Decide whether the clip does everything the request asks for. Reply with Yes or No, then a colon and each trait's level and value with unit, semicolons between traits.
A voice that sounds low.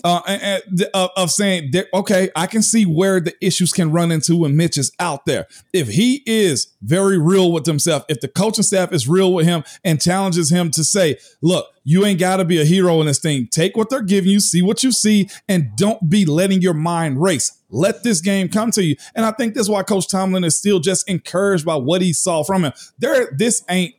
No: medium, 185 Hz